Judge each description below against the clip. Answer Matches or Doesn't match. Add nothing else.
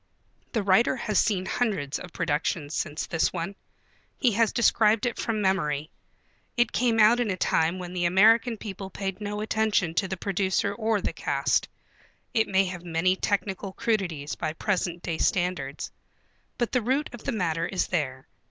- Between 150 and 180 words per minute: Matches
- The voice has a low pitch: Doesn't match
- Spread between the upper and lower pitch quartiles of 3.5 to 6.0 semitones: Matches